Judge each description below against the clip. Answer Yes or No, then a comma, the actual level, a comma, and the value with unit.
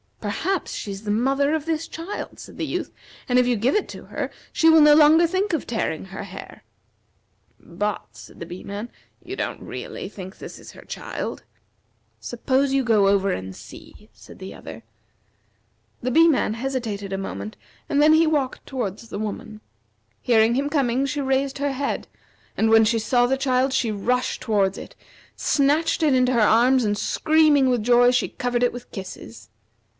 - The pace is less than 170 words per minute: No, average, 185 wpm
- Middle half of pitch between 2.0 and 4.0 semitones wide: No, average, 5.2 semitones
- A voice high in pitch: Yes, high, 245 Hz